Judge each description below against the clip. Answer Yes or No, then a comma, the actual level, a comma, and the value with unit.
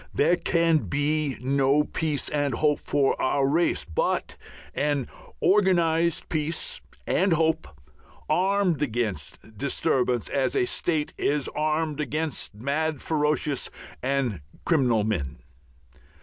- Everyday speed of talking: No, slow, 110 wpm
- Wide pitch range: No, average, 3.2 semitones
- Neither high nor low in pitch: Yes, medium, 150 Hz